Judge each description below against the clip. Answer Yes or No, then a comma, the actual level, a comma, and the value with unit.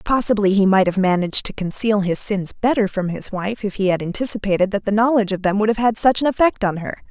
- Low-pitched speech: No, high, 205 Hz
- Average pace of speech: No, fast, 255 wpm